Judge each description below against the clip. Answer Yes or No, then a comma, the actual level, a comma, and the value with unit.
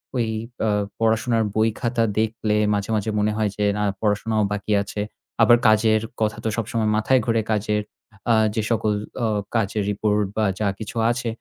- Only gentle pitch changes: Yes, narrow, 1.2 semitones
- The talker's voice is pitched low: Yes, low, 110 Hz